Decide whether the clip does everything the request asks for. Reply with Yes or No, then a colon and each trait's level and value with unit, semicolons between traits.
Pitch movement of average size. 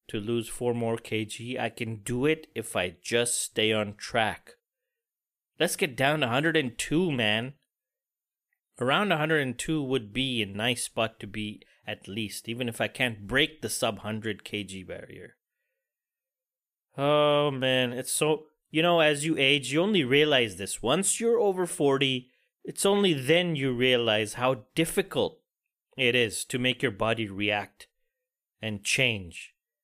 No: wide, 6.1 semitones